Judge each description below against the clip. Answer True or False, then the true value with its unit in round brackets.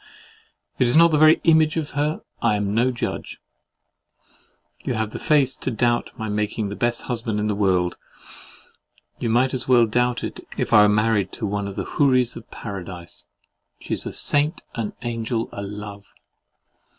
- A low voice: True (115 Hz)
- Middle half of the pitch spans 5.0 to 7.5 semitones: False (3.7 semitones)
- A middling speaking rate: True (180 wpm)